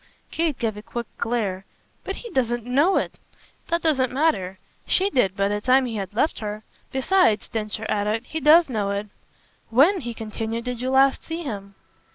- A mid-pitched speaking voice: No, high, 240 Hz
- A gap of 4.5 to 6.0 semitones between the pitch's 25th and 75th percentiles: Yes, average, 5.2 semitones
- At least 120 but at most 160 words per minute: No, average, 185 wpm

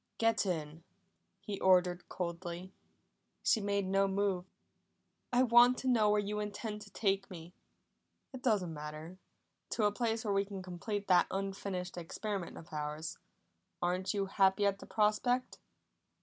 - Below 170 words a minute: Yes, average, 150 wpm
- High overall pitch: Yes, high, 195 Hz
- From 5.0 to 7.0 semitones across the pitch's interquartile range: No, average, 2.8 semitones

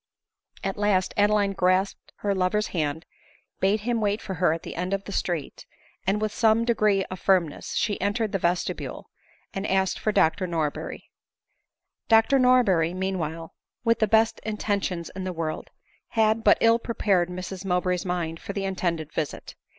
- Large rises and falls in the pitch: No, average, 3.0 semitones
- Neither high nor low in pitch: No, high, 195 Hz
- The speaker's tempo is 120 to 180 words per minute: Yes, average, 165 wpm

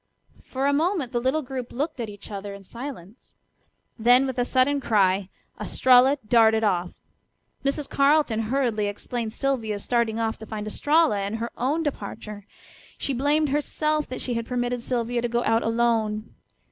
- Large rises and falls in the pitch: No, average, 3.9 semitones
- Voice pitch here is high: Yes, high, 240 Hz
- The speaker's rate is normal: Yes, average, 165 wpm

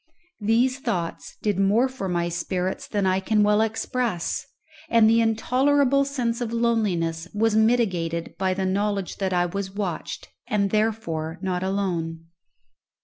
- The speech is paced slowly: No, average, 145 wpm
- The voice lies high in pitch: Yes, high, 200 Hz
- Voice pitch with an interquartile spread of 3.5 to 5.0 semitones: Yes, average, 3.9 semitones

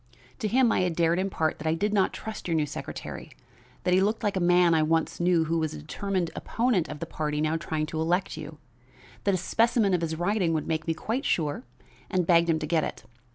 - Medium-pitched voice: Yes, medium, 170 Hz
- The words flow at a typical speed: No, fast, 240 wpm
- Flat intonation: No, average, 3.5 semitones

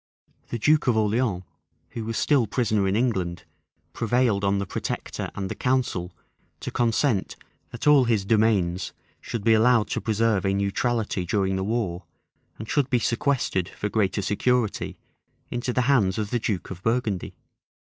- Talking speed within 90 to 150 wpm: No, average, 160 wpm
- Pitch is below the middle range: Yes, low, 110 Hz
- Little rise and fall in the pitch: No, average, 3.7 semitones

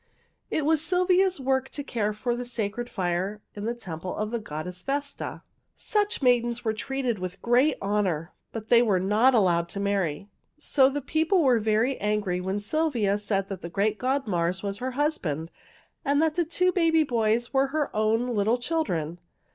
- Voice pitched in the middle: No, high, 230 Hz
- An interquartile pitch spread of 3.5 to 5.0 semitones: No, wide, 5.6 semitones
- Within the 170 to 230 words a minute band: Yes, average, 175 wpm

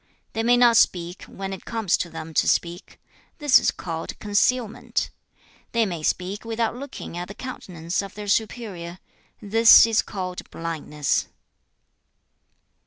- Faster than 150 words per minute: No, average, 140 wpm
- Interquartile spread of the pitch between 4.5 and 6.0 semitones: Yes, average, 4.9 semitones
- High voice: Yes, high, 200 Hz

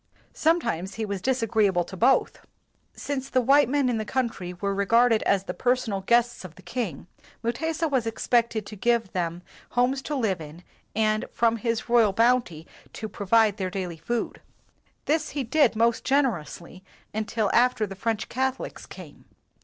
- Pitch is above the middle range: Yes, high, 225 Hz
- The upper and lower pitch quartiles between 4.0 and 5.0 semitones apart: Yes, average, 4.3 semitones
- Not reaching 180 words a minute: Yes, average, 165 wpm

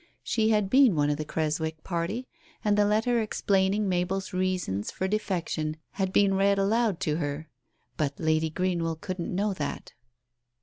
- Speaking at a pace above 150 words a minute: Yes, average, 160 wpm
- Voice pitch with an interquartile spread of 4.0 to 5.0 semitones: Yes, average, 4.4 semitones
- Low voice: No, medium, 185 Hz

